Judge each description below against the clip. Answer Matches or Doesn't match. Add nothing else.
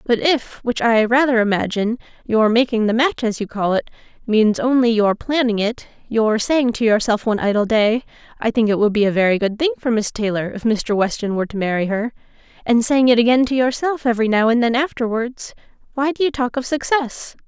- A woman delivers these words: Matches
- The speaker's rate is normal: Doesn't match